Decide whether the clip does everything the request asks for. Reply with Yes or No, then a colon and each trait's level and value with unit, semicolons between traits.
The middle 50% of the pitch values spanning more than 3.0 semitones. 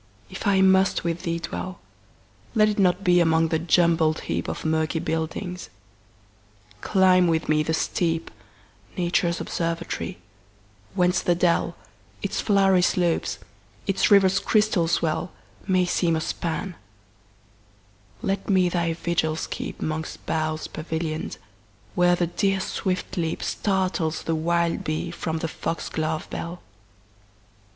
No: narrow, 2.5 semitones